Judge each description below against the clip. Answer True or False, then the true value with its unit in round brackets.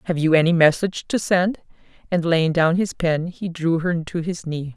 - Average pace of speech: False (215 wpm)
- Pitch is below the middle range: False (170 Hz)